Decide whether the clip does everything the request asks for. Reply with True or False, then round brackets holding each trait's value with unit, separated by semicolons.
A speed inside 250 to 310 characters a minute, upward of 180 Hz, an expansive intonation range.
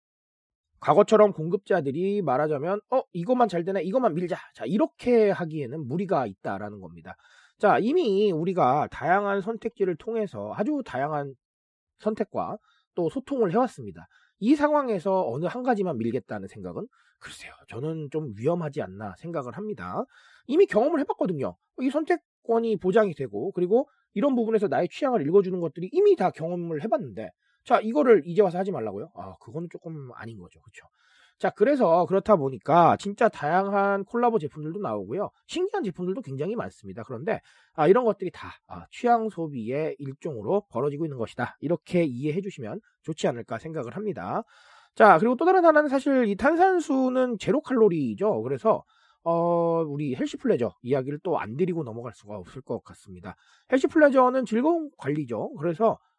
False (370 characters per minute; 190 Hz; 7.8 semitones)